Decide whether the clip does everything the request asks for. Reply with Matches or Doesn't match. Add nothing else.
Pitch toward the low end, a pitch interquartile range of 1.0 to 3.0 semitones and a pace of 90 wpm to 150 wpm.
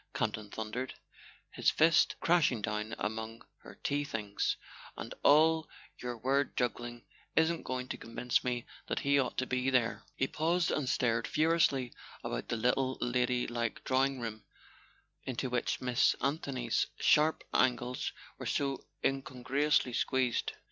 Matches